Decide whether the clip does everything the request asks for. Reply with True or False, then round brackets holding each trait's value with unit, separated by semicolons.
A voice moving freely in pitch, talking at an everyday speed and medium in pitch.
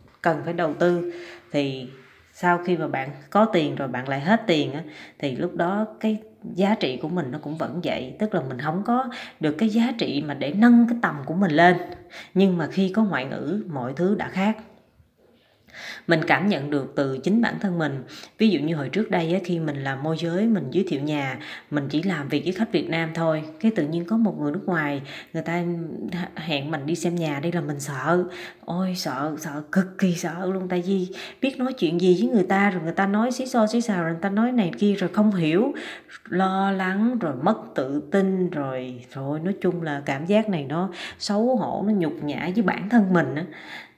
False (4.7 semitones; 230 wpm; 175 Hz)